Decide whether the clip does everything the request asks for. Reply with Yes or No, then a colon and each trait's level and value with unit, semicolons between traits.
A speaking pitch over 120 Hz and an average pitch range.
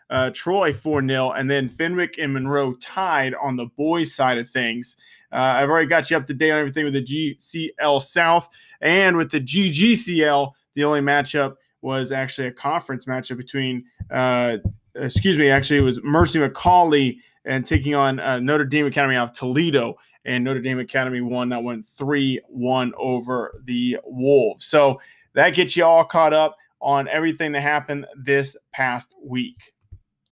Yes: medium, 140 Hz; average, 3.2 semitones